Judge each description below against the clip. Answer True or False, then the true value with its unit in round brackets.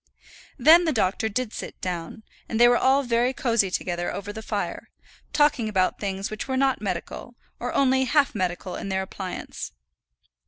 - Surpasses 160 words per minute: True (170 wpm)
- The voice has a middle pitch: False (220 Hz)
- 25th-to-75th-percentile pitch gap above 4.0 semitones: True (5.4 semitones)